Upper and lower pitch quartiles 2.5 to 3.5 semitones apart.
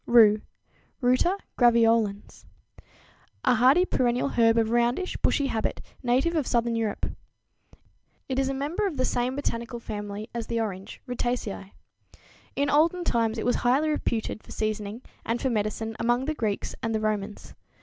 Yes: average, 3.2 semitones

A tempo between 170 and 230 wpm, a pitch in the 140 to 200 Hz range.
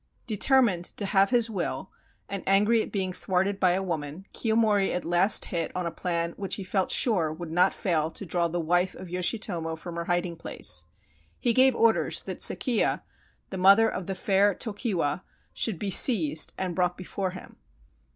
Yes: average, 180 wpm; medium, 185 Hz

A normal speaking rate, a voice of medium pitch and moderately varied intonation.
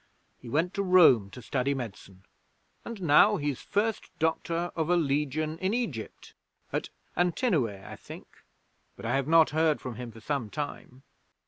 No: average, 160 wpm; medium, 150 Hz; wide, 5.7 semitones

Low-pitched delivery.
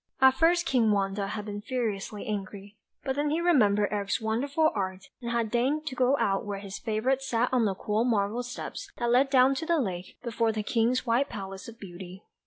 No: high, 230 Hz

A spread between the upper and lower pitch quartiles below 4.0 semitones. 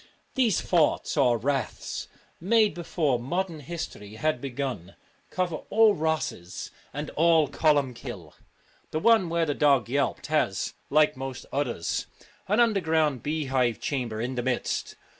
No: average, 4.9 semitones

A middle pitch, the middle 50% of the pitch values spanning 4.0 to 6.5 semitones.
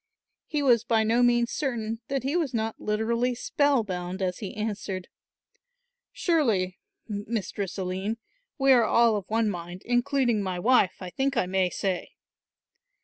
No: high, 220 Hz; average, 4.4 semitones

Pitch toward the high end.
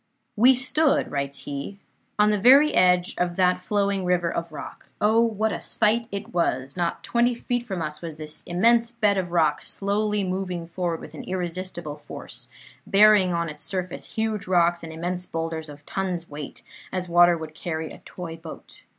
No: medium, 180 Hz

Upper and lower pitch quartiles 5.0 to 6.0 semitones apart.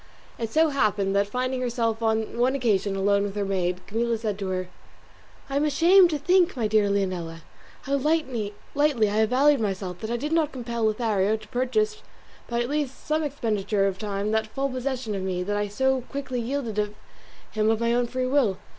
No: average, 4.5 semitones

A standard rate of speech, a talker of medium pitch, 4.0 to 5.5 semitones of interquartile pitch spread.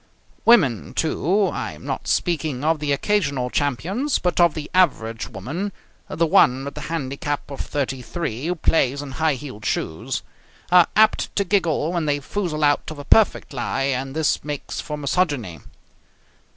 Yes: average, 165 wpm; medium, 150 Hz; average, 4.3 semitones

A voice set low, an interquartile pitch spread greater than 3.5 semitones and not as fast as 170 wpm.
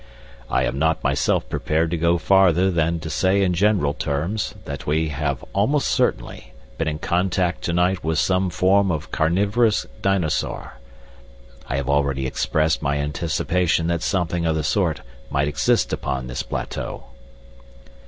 Yes: very low, 80 Hz; average, 3.9 semitones; average, 155 wpm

